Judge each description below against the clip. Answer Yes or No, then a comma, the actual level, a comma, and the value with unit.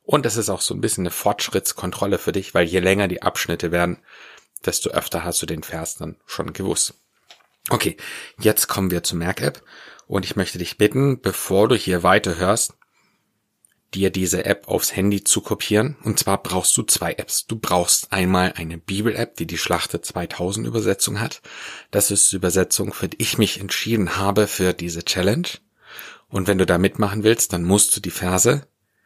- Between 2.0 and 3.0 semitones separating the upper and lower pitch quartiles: Yes, average, 2.7 semitones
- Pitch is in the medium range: No, very low, 95 Hz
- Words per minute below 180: No, average, 185 wpm